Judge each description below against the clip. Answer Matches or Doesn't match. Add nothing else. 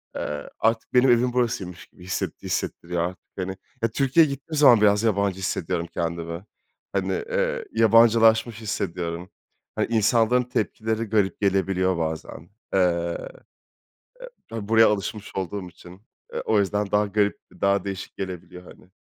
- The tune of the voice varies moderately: Matches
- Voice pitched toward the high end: Doesn't match